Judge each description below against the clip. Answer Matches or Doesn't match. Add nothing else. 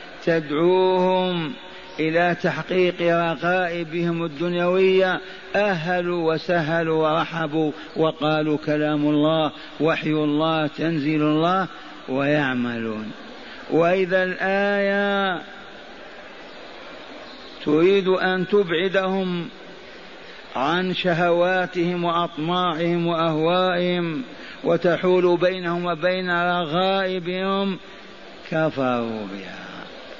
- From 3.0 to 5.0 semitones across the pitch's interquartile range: Doesn't match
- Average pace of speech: Doesn't match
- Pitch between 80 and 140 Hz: Doesn't match